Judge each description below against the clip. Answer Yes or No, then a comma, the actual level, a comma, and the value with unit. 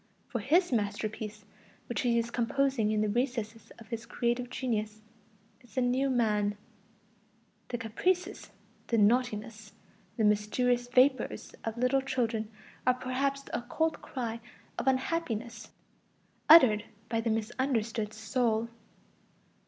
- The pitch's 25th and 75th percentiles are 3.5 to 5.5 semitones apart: No, average, 2.8 semitones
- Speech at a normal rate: No, slow, 120 wpm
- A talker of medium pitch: No, high, 235 Hz